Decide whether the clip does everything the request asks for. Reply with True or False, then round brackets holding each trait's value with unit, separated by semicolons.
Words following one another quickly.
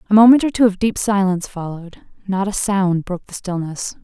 True (210 wpm)